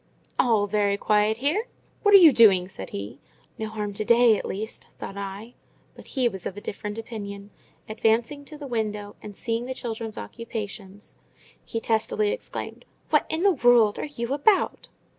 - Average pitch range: Yes, average, 3.2 semitones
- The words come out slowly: No, average, 170 wpm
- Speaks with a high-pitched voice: Yes, high, 220 Hz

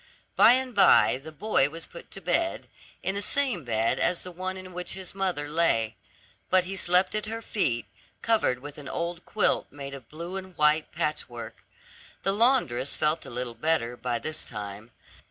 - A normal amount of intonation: No, wide, 6.8 semitones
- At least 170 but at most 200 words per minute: Yes, average, 185 wpm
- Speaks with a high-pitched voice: No, medium, 165 Hz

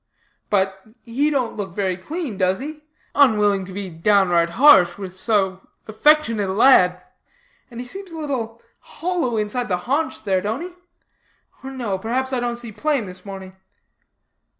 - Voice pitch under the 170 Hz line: No, high, 220 Hz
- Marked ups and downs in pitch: Yes, wide, 5.7 semitones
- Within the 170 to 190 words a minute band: No, average, 160 wpm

